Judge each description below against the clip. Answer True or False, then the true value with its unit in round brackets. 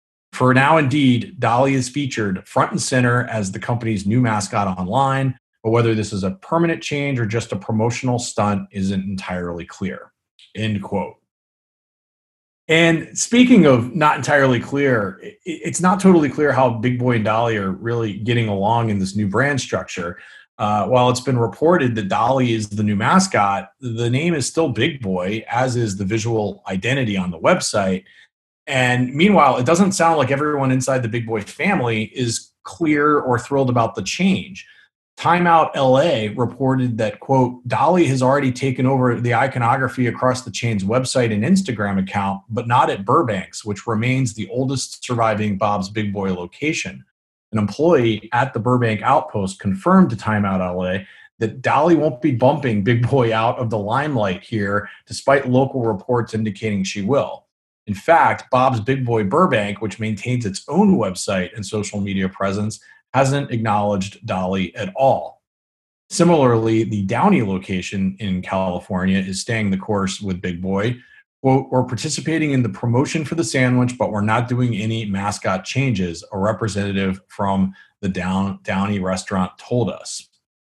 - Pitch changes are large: False (4.6 semitones)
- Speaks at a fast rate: False (160 wpm)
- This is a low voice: True (115 Hz)